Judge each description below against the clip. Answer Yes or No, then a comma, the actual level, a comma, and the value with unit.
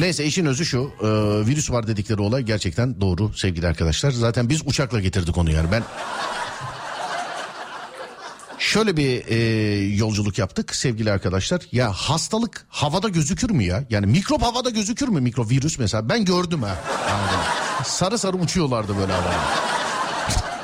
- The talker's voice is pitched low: Yes, low, 125 Hz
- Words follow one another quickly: Yes, fast, 145 wpm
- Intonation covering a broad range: Yes, wide, 7.7 semitones